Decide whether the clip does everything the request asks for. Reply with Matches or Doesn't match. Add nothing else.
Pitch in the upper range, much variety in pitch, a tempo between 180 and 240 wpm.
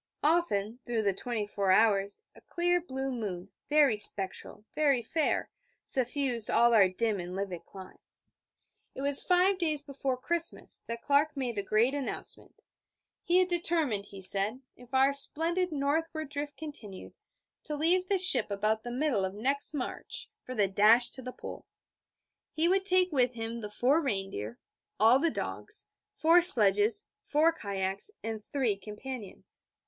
Doesn't match